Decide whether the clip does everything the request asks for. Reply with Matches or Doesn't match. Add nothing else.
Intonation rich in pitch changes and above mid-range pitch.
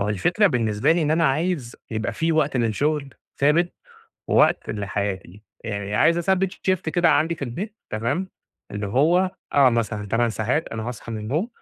Doesn't match